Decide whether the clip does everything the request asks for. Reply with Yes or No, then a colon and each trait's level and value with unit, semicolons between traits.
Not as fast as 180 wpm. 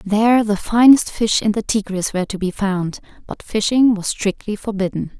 No: average, 185 wpm